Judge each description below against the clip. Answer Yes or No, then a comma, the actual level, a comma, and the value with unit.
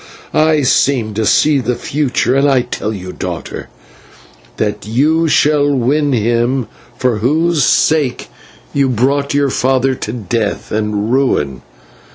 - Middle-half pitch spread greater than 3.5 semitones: Yes, average, 4.3 semitones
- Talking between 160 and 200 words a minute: No, slow, 135 wpm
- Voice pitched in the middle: No, low, 130 Hz